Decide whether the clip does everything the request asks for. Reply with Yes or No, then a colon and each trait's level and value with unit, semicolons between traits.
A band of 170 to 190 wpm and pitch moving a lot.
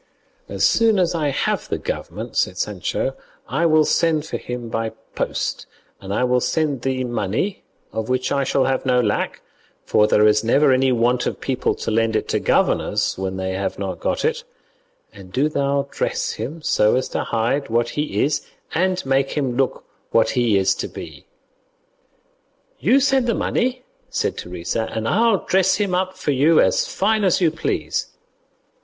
Yes: average, 180 wpm; wide, 6.6 semitones